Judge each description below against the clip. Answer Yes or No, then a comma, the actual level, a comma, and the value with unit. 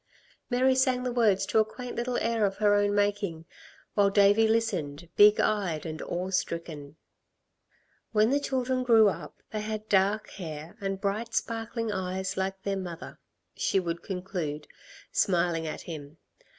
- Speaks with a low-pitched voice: No, high, 200 Hz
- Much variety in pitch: No, average, 4.0 semitones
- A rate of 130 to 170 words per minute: Yes, average, 155 wpm